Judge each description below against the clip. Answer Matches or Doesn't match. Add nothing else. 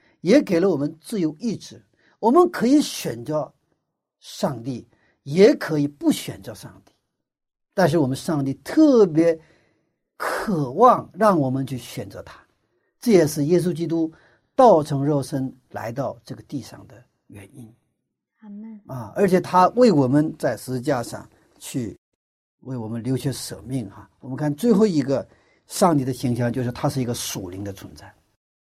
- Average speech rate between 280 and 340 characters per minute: Doesn't match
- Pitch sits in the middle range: Matches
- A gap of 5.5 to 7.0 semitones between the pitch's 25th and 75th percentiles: Matches